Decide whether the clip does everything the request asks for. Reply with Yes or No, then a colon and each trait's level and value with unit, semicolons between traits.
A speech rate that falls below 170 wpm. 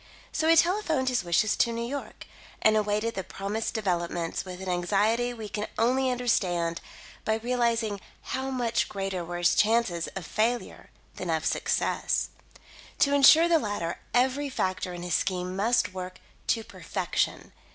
Yes: average, 155 wpm